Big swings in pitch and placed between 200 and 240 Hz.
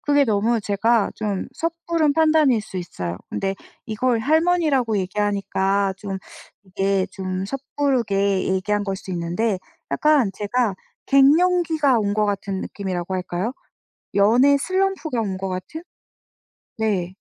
Yes: wide, 6.5 semitones; high, 210 Hz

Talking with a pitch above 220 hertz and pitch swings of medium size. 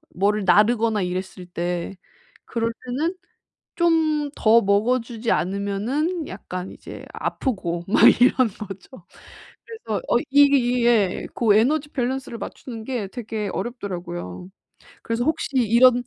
Yes: high, 230 Hz; average, 4.5 semitones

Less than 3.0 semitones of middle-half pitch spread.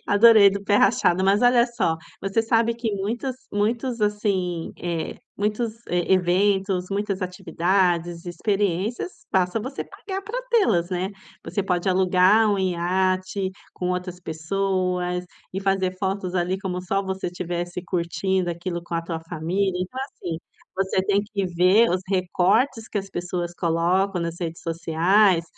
Yes: narrow, 2.5 semitones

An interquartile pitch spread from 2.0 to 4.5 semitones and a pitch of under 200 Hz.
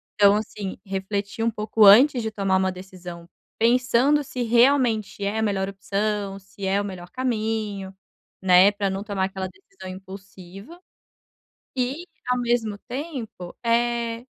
No: average, 3.7 semitones; high, 205 Hz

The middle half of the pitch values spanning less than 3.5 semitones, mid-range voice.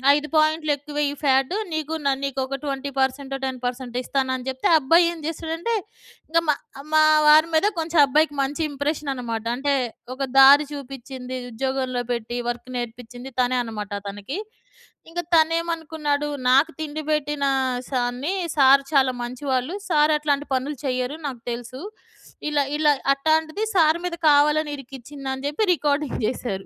No: average, 3.0 semitones; very high, 280 Hz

